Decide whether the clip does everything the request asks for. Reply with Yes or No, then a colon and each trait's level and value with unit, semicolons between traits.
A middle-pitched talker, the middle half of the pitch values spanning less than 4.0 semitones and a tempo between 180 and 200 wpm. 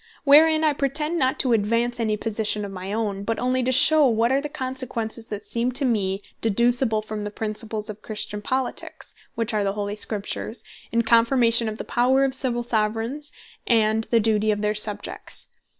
No: high, 230 Hz; average, 3.3 semitones; average, 185 wpm